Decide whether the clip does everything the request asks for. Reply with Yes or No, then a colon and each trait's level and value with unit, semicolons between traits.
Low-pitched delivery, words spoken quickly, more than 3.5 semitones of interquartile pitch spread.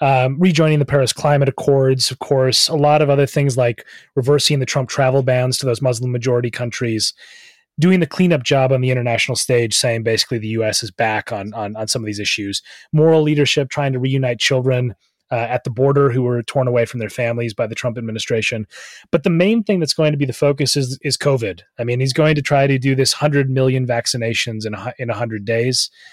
No: low, 130 Hz; fast, 220 wpm; average, 3.2 semitones